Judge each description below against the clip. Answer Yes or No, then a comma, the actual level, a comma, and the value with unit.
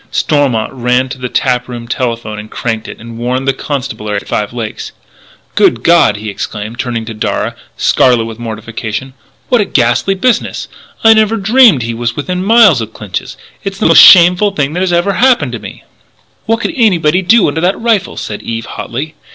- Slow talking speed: No, average, 185 wpm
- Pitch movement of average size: No, wide, 8.4 semitones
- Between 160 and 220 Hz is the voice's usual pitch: No, low, 130 Hz